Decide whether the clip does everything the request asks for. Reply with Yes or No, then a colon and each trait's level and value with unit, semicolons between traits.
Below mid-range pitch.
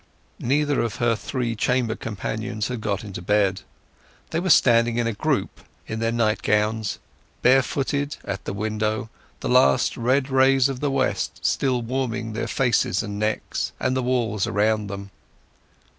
Yes: low, 115 Hz